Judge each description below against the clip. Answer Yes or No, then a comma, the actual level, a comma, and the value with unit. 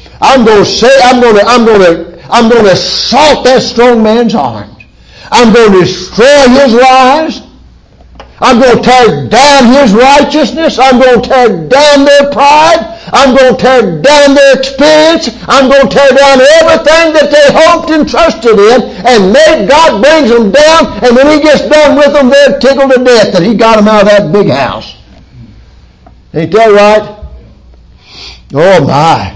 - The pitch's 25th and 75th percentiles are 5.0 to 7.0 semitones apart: No, average, 4.0 semitones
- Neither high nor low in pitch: No, very high, 260 Hz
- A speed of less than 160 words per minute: No, average, 175 wpm